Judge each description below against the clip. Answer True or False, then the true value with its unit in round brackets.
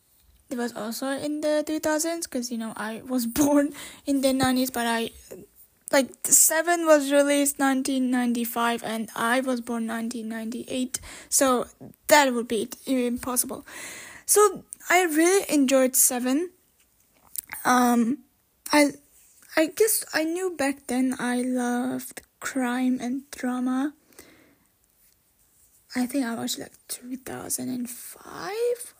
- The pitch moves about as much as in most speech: True (3.4 semitones)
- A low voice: False (260 Hz)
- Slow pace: True (130 wpm)